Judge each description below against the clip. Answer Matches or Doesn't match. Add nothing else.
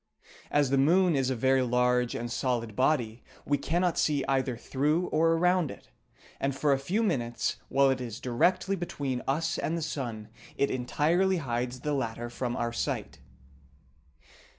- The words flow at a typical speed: Matches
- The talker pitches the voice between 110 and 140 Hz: Matches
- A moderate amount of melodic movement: Matches